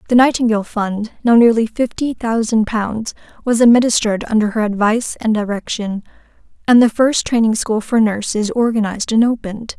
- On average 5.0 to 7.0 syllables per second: Yes, 5.5 syllables/s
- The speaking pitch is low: No, high, 225 Hz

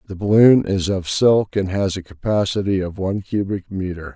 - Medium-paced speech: Yes, average, 190 wpm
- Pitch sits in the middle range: No, very low, 95 Hz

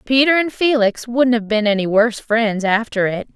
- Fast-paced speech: No, average, 195 wpm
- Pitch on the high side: Yes, high, 230 Hz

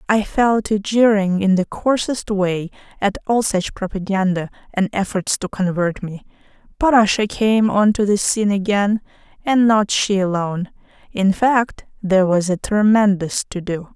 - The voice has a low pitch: No, high, 200 Hz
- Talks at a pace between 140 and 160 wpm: Yes, average, 155 wpm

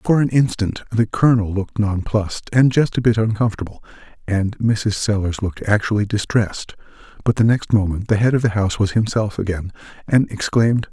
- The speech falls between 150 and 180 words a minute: Yes, average, 175 wpm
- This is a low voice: Yes, low, 105 Hz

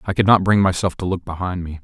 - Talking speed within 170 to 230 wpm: No, fast, 295 wpm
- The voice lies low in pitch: Yes, very low, 90 Hz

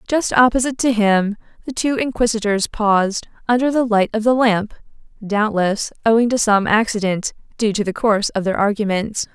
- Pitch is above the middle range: Yes, high, 220 Hz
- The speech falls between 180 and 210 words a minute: No, average, 160 wpm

